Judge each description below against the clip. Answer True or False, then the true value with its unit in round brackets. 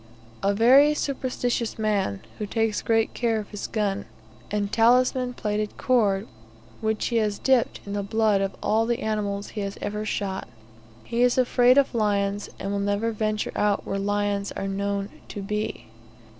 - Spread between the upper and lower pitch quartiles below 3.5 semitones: True (2.4 semitones)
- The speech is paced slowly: False (170 wpm)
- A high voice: True (210 Hz)